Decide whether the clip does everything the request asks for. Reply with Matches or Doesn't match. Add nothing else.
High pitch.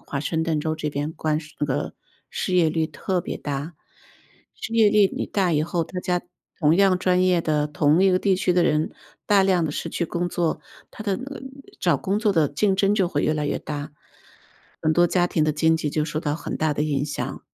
Doesn't match